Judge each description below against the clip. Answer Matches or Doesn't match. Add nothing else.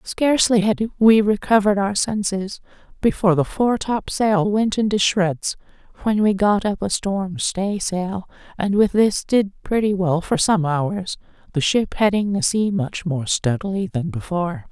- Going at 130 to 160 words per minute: Matches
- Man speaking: Doesn't match